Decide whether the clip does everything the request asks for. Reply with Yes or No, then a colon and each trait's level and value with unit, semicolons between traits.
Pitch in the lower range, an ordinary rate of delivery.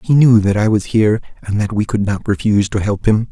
No: low, 105 Hz; fast, 270 wpm